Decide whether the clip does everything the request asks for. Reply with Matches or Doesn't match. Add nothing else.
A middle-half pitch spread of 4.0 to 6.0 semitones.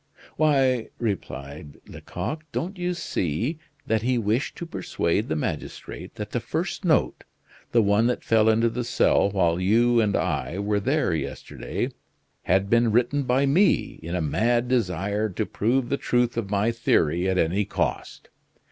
Matches